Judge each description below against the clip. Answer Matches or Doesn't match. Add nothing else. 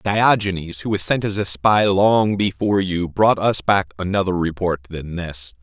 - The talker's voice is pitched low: Matches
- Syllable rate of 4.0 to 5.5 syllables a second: Matches